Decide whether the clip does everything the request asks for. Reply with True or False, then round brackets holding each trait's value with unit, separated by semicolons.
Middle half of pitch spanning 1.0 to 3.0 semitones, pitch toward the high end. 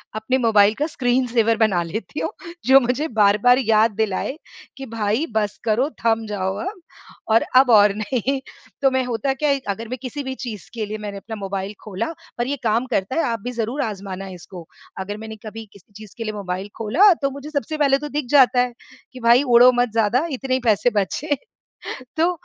False (3.9 semitones; 230 Hz)